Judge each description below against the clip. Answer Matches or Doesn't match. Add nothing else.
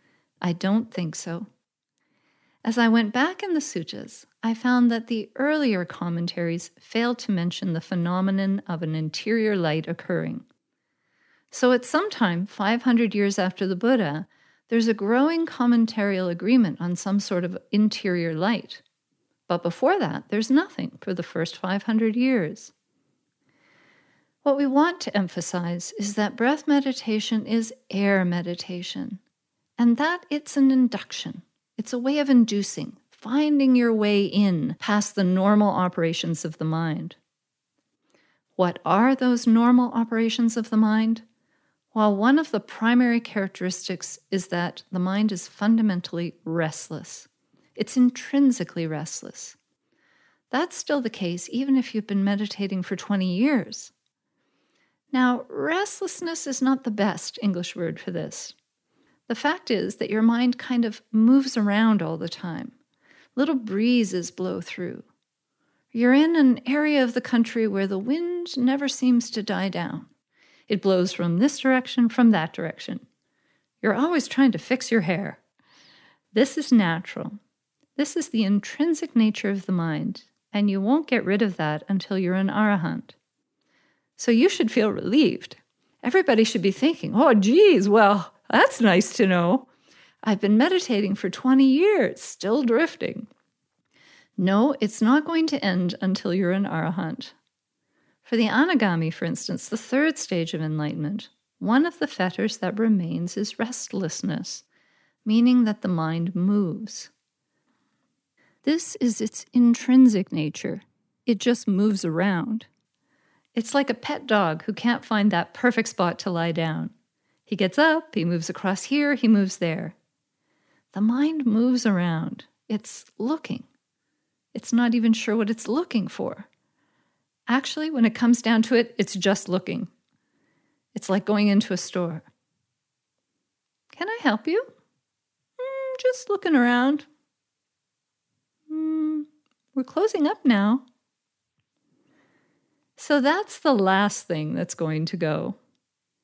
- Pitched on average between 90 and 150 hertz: Doesn't match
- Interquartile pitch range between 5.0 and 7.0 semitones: Matches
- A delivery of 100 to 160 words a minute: Matches